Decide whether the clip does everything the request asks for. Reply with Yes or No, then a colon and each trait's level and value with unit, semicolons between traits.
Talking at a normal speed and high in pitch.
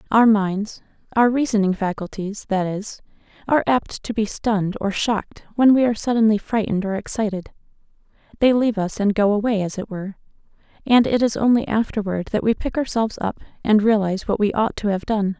Yes: average, 180 wpm; high, 210 Hz